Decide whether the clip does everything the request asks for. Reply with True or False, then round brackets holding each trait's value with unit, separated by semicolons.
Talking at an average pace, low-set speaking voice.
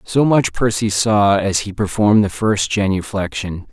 True (160 wpm; 100 Hz)